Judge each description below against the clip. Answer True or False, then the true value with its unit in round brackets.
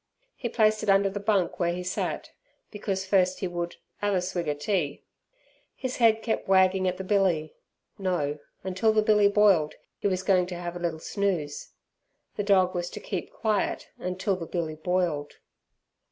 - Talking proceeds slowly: False (180 wpm)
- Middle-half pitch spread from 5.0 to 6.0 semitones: False (2.6 semitones)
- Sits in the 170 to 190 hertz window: True (185 Hz)